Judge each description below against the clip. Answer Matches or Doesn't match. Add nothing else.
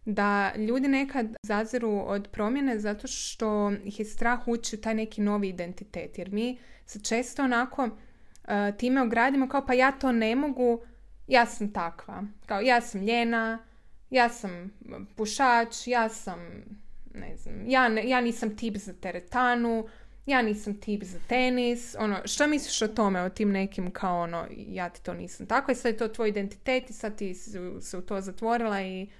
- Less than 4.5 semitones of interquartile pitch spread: Matches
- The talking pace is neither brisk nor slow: Doesn't match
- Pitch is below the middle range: Doesn't match